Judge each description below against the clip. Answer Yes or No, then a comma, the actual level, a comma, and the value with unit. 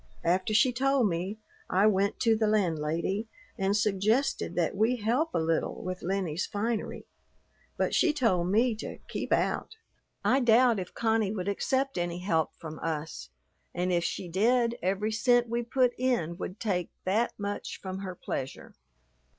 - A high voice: Yes, high, 205 Hz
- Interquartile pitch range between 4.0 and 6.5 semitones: Yes, average, 4.6 semitones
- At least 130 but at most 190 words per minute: Yes, average, 160 wpm